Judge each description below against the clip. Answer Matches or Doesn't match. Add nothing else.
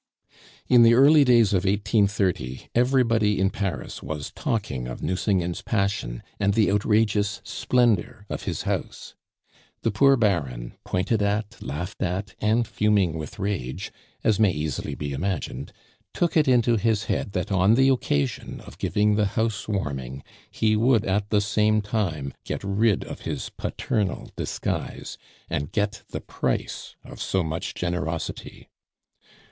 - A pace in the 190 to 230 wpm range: Doesn't match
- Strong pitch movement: Doesn't match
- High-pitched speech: Doesn't match